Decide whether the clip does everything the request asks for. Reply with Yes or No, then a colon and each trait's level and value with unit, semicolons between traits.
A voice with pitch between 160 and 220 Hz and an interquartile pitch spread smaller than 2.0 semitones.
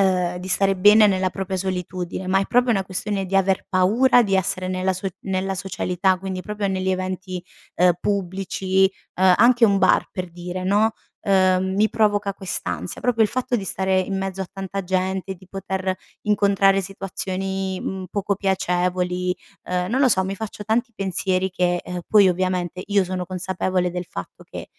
Yes: high, 190 Hz; narrow, 1.2 semitones